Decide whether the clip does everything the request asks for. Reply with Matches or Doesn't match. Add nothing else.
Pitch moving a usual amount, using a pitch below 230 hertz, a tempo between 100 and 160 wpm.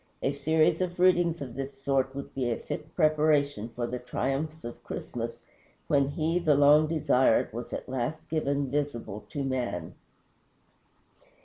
Matches